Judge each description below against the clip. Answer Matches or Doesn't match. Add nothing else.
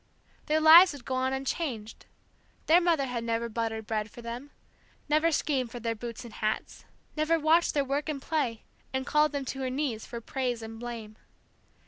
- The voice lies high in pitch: Matches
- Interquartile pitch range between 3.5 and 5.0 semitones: Matches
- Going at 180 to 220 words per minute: Matches